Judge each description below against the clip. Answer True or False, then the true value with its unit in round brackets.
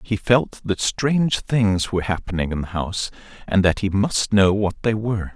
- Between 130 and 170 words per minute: False (200 wpm)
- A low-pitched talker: True (105 Hz)